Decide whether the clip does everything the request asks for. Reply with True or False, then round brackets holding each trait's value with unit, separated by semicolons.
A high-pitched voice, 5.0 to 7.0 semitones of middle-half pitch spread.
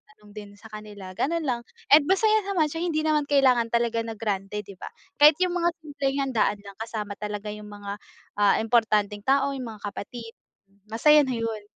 True (230 Hz; 5.5 semitones)